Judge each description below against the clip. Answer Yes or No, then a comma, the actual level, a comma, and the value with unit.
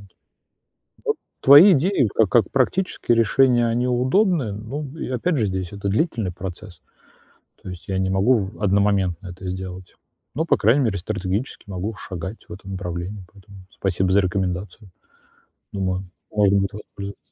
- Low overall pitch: Yes, low, 100 Hz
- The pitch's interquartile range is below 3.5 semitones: No, average, 4.2 semitones